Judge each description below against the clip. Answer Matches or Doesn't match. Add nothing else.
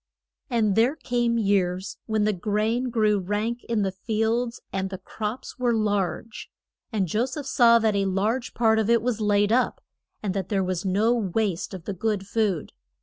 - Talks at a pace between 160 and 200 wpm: Matches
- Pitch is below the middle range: Doesn't match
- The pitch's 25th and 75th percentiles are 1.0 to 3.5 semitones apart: Matches